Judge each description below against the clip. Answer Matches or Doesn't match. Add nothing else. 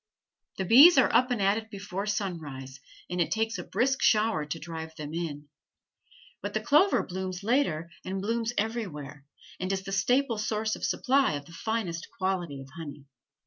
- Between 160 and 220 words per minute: Matches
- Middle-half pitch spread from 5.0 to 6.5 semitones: Matches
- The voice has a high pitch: Matches